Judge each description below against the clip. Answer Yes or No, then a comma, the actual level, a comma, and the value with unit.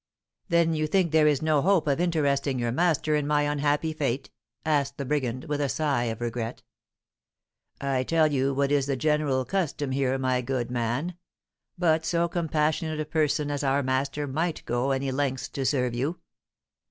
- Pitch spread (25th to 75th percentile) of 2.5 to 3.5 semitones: Yes, average, 2.9 semitones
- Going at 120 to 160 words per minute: No, average, 175 wpm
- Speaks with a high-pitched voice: No, medium, 145 Hz